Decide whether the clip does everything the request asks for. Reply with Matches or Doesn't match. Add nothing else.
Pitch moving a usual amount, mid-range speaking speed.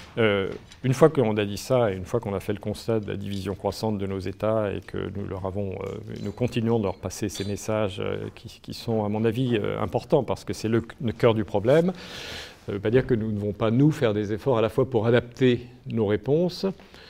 Doesn't match